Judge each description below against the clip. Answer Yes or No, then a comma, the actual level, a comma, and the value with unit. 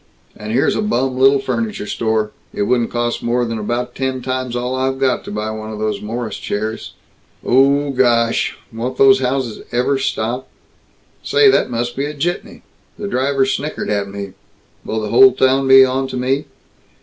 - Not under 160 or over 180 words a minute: Yes, average, 175 wpm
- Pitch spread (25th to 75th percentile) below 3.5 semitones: Yes, average, 2.9 semitones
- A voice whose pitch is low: Yes, low, 125 Hz